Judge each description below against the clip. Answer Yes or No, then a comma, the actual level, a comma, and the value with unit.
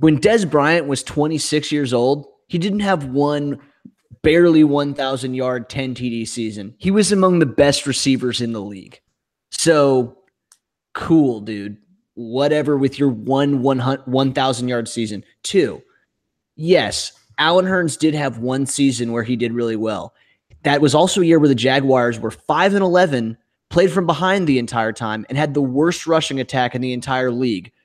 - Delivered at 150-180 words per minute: Yes, average, 160 wpm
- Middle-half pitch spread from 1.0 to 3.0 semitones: No, average, 4.1 semitones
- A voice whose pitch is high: No, low, 135 Hz